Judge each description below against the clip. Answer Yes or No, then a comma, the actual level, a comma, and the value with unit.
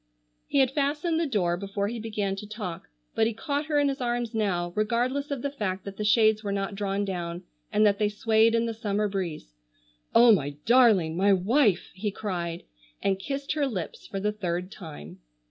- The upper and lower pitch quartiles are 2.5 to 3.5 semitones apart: No, average, 3.9 semitones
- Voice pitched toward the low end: No, high, 210 Hz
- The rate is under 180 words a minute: No, average, 200 wpm